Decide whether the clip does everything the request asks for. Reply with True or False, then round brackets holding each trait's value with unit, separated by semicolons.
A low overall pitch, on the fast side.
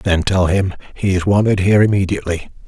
False (95 Hz; 180 wpm)